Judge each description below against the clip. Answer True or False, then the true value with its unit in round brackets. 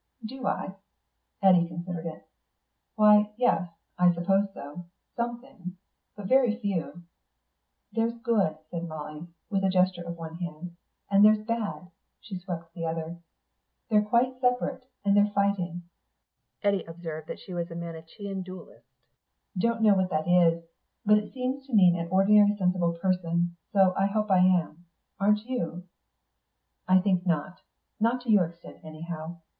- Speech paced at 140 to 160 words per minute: True (150 wpm)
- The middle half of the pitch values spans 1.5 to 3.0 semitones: False (3.6 semitones)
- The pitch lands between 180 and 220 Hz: True (185 Hz)